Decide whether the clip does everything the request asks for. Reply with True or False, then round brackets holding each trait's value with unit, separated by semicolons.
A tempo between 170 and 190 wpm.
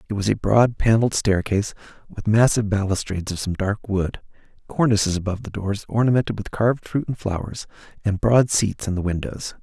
True (180 wpm)